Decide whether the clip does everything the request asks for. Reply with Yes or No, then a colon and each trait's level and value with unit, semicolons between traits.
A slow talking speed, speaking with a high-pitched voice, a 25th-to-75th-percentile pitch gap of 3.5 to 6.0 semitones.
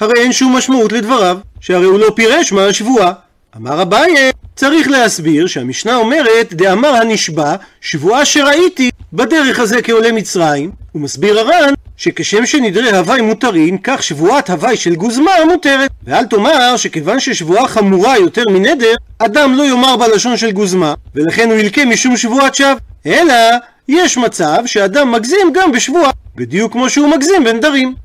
No: average, 145 wpm; high, 230 Hz; wide, 5.5 semitones